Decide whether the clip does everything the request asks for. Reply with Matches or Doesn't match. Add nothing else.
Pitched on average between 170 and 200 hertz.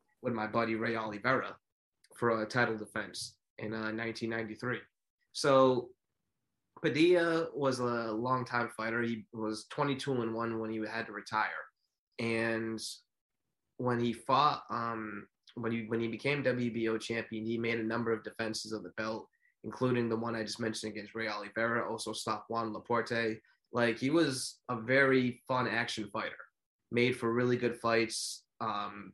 Doesn't match